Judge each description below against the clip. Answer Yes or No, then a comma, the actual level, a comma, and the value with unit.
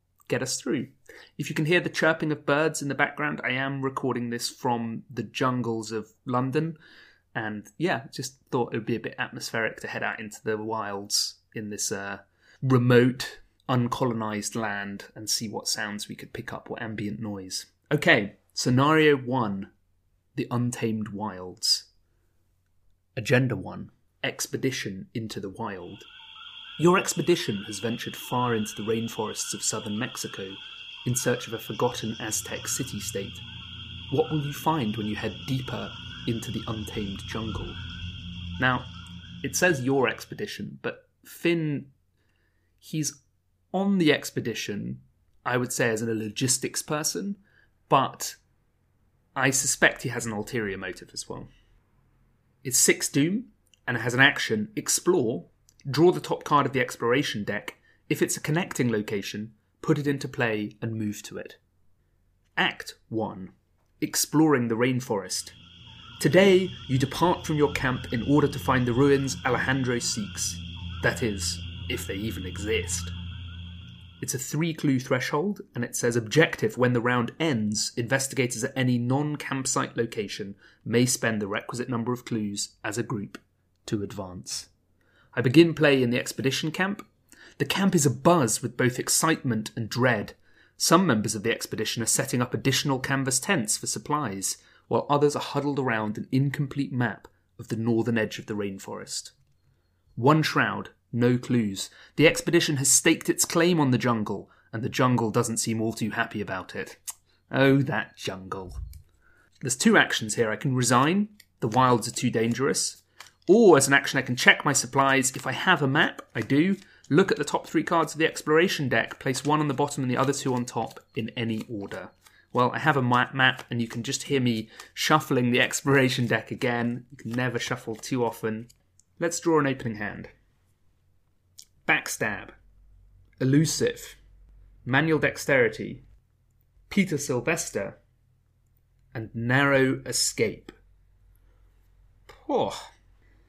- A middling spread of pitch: Yes, average, 4.9 semitones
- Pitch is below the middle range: Yes, low, 120 Hz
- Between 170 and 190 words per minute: No, average, 155 wpm